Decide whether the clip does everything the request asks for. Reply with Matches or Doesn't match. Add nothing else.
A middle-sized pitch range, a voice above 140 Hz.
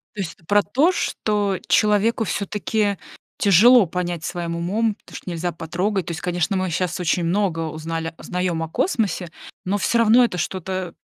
Matches